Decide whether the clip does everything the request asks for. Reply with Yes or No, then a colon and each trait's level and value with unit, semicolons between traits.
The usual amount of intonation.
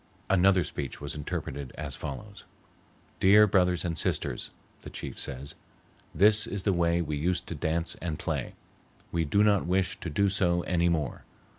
Yes: average, 4.0 semitones